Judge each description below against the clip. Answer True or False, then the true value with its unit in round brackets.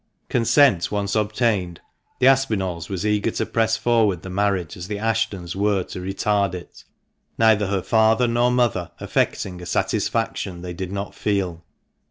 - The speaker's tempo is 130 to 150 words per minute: False (160 wpm)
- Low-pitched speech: True (100 Hz)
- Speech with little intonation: False (3.5 semitones)